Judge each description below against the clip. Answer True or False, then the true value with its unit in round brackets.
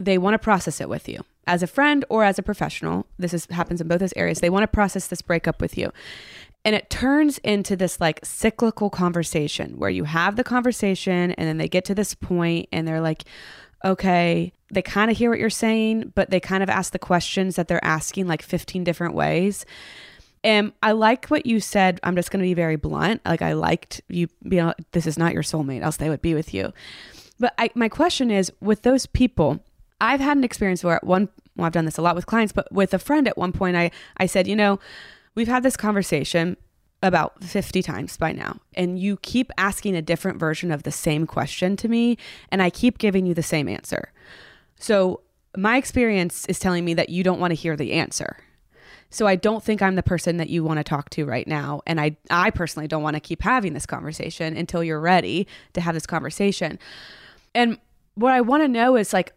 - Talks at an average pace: False (225 wpm)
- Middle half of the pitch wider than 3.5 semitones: True (4.1 semitones)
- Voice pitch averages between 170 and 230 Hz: True (185 Hz)